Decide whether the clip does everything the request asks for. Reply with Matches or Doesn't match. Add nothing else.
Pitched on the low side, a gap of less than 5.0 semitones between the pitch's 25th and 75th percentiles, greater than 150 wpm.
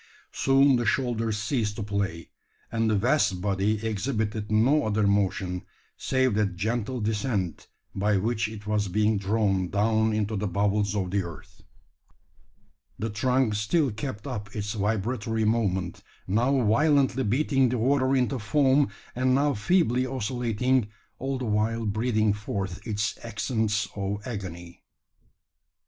Doesn't match